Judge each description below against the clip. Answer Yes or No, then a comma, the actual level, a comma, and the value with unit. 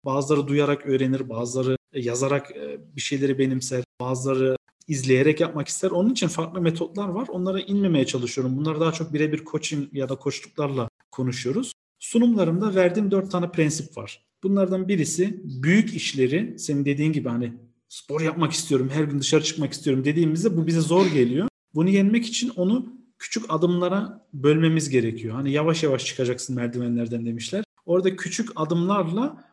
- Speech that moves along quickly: Yes, fast, 150 wpm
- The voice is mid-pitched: Yes, medium, 155 Hz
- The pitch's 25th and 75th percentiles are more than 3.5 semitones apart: Yes, wide, 5.6 semitones